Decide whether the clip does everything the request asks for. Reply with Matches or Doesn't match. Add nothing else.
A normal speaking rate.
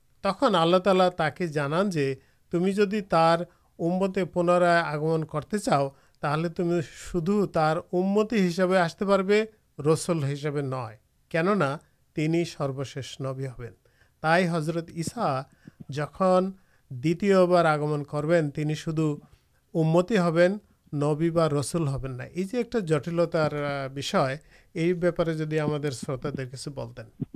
Doesn't match